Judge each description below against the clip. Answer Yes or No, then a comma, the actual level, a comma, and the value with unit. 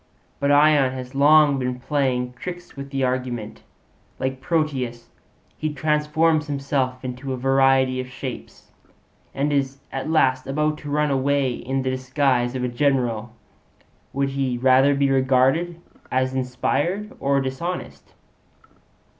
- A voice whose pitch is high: No, low, 135 Hz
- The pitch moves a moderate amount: No, narrow, 2.1 semitones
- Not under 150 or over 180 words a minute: No, slow, 135 wpm